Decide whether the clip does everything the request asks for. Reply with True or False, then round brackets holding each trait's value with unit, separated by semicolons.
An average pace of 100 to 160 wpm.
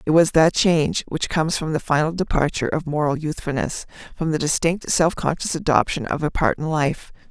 False (190 wpm)